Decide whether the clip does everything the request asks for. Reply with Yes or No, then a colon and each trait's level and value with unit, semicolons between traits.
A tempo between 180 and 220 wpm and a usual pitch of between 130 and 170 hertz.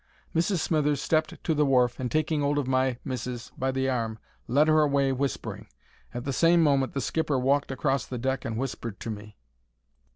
Yes: average, 200 wpm; low, 135 Hz